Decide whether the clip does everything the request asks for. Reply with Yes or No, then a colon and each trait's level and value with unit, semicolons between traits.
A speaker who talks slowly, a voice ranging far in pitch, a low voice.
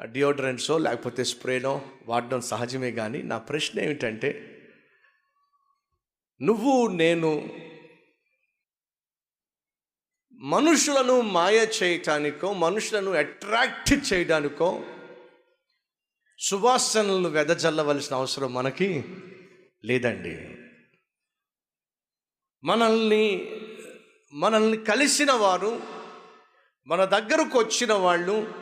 No: slow, 65 wpm; wide, 8.8 semitones; high, 190 Hz